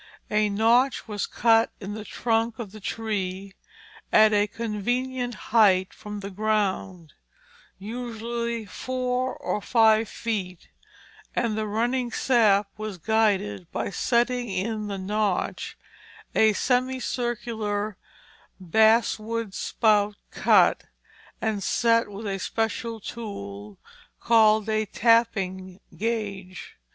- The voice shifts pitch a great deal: No, narrow, 2.5 semitones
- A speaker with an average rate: No, slow, 105 wpm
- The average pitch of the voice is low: No, high, 215 Hz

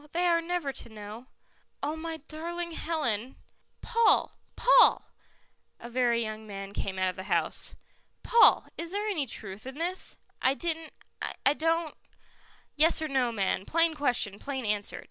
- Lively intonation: Yes, wide, 7.2 semitones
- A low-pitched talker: No, very high, 280 Hz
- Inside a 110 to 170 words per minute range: Yes, average, 165 wpm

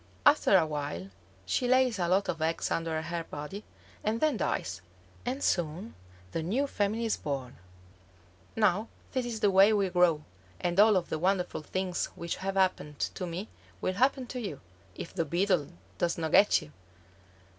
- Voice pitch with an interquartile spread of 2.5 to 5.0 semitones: Yes, average, 4.6 semitones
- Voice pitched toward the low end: No, medium, 185 Hz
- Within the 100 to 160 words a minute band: No, average, 175 wpm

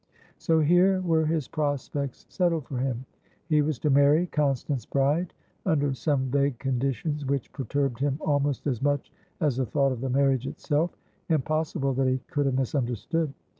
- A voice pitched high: No, medium, 140 Hz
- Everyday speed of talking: Yes, average, 160 wpm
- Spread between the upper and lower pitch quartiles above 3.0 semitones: No, narrow, 2.6 semitones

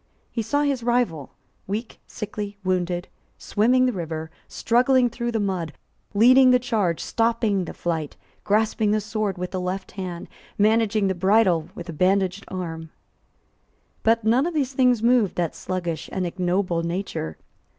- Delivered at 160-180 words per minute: No, average, 150 wpm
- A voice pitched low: No, high, 200 Hz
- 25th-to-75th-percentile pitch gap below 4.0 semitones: No, average, 4.5 semitones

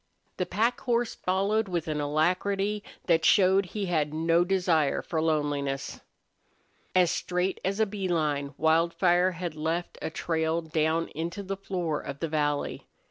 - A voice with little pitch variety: No, average, 3.3 semitones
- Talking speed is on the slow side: No, average, 150 wpm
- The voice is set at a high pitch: No, medium, 170 Hz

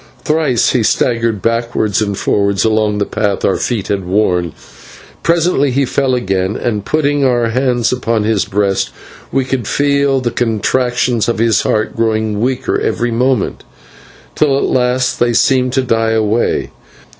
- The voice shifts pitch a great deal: No, average, 3.3 semitones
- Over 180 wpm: No, average, 155 wpm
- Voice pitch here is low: Yes, low, 115 Hz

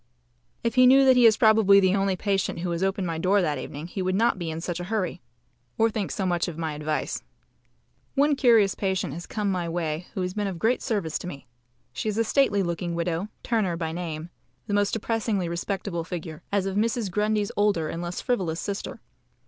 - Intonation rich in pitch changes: No, average, 3.7 semitones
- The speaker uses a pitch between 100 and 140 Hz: No, high, 190 Hz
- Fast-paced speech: Yes, fast, 215 wpm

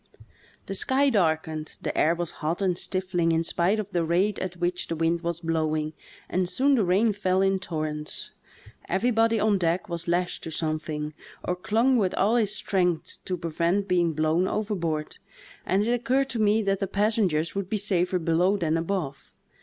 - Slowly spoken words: No, average, 180 wpm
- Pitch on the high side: No, medium, 180 Hz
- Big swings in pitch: No, average, 3.7 semitones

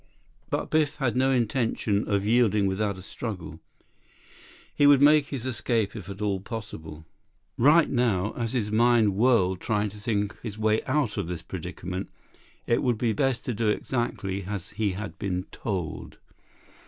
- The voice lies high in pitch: No, low, 110 Hz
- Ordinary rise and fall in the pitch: Yes, average, 3.7 semitones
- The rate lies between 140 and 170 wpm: Yes, average, 165 wpm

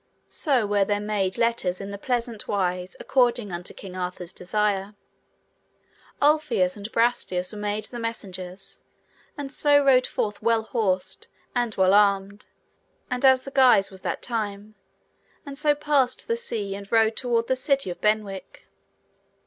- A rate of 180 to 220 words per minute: No, average, 150 wpm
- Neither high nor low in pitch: No, high, 215 Hz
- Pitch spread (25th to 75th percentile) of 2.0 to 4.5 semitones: Yes, average, 4.2 semitones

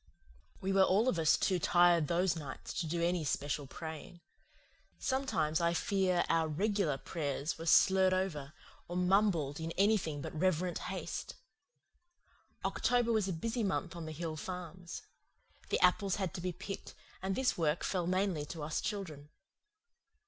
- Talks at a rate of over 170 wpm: No, average, 155 wpm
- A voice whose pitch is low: No, medium, 175 Hz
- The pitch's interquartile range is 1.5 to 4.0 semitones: Yes, average, 3.3 semitones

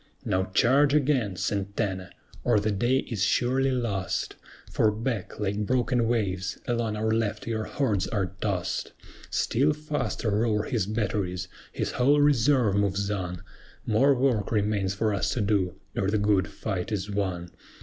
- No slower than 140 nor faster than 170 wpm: Yes, average, 150 wpm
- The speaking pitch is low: Yes, low, 105 Hz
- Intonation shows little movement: No, average, 3.6 semitones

